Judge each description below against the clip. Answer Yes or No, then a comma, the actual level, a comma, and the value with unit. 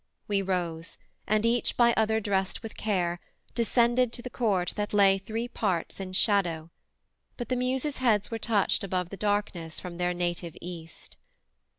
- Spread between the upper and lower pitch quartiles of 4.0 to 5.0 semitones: Yes, average, 4.3 semitones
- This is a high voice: Yes, high, 200 Hz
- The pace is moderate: Yes, average, 165 wpm